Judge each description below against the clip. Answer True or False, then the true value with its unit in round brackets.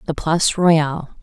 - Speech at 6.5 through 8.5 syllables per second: False (5.0 syllables/s)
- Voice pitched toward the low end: False (160 Hz)